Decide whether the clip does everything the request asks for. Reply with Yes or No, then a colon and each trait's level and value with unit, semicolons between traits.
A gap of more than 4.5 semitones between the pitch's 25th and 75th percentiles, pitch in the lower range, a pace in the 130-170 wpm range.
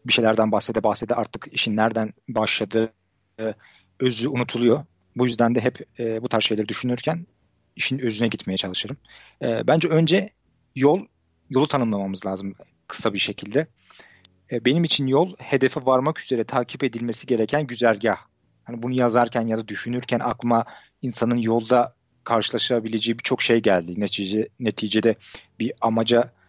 No: narrow, 2.6 semitones; low, 115 Hz; fast, 140 wpm